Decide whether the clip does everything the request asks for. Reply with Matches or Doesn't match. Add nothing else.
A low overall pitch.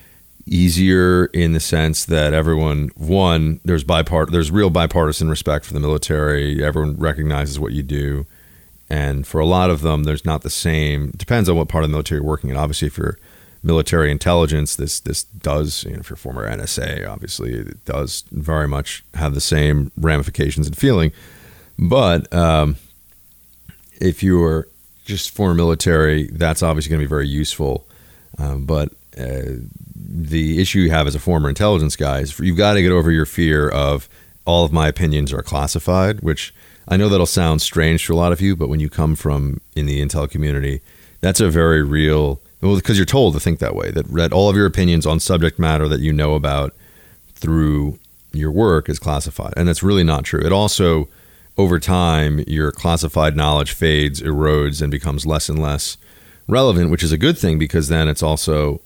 Matches